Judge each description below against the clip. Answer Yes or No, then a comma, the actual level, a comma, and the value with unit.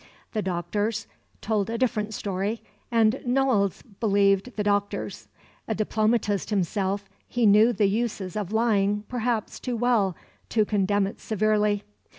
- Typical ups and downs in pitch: No, narrow, 2.1 semitones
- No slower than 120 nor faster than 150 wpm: Yes, slow, 135 wpm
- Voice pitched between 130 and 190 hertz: No, high, 210 Hz